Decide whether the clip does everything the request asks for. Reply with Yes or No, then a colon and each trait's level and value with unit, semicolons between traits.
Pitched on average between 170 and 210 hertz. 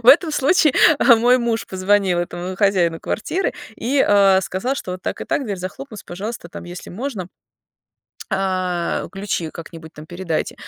Yes: high, 190 Hz